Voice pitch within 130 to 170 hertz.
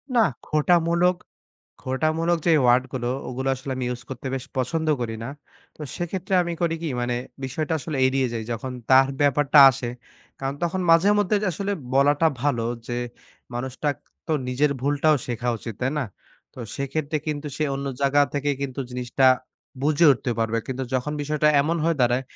Yes: medium, 140 Hz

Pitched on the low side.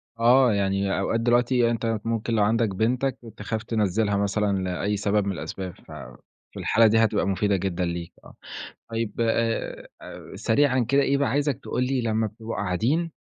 Yes: low, 110 Hz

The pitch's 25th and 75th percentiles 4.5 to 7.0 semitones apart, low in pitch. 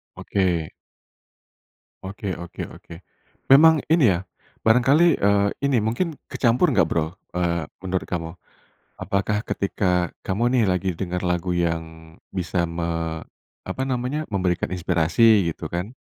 Yes: average, 4.8 semitones; very low, 95 Hz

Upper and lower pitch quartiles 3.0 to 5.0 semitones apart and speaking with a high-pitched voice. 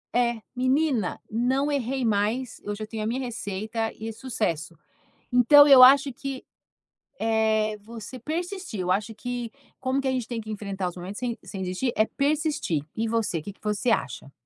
Yes: average, 3.7 semitones; high, 230 Hz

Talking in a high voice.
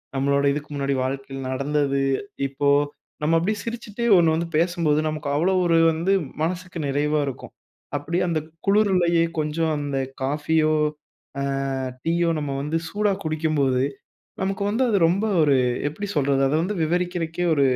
No: medium, 160 Hz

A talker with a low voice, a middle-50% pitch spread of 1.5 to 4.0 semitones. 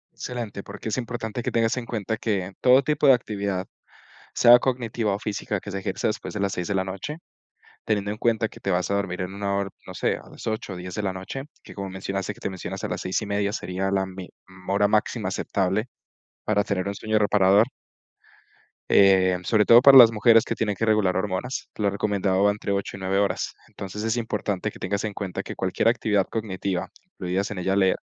Yes: low, 100 Hz; narrow, 2.5 semitones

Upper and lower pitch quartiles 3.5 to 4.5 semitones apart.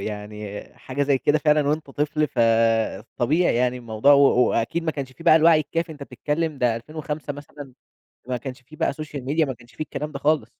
Yes: average, 4.2 semitones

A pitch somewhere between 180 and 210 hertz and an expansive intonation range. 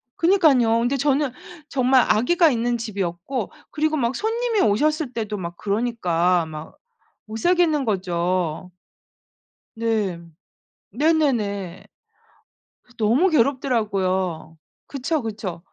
No: high, 230 Hz; wide, 6.9 semitones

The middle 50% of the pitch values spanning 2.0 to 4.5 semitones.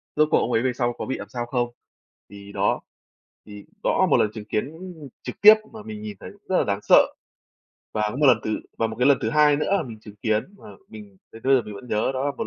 No: average, 5.1 semitones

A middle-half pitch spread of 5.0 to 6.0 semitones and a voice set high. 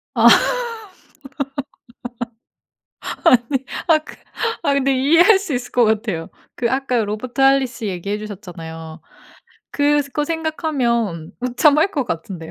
Yes: wide, 5.6 semitones; very high, 250 Hz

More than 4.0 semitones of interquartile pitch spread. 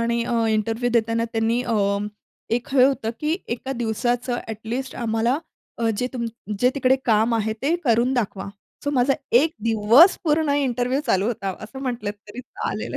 No: narrow, 2.5 semitones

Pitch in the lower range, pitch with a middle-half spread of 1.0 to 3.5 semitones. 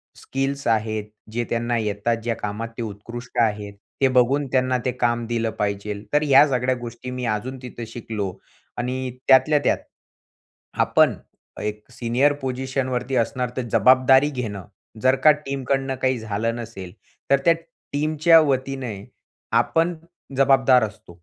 Yes: low, 125 Hz; average, 3.0 semitones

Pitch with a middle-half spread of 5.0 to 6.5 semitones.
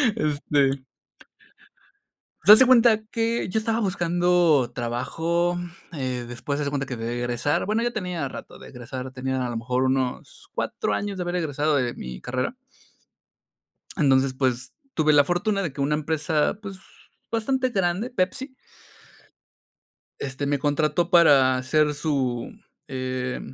Yes: wide, 5.6 semitones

